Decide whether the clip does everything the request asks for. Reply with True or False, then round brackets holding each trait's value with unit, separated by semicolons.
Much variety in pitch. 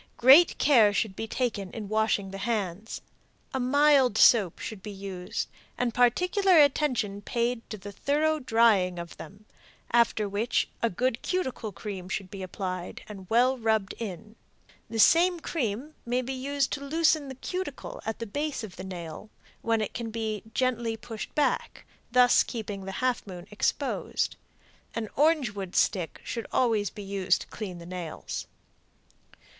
False (4.5 semitones)